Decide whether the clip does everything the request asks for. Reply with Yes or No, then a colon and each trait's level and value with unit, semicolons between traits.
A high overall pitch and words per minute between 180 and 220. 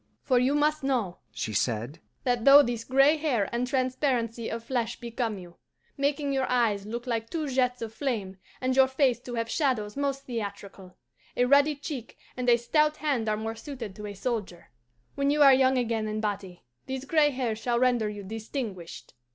Yes: high, 245 Hz; average, 190 wpm